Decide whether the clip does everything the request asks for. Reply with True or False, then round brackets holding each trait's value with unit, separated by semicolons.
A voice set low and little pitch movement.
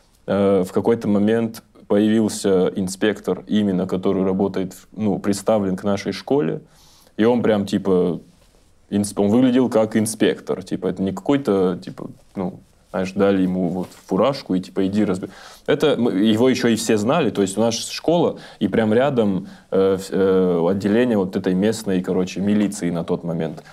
True (100 Hz; 2.3 semitones)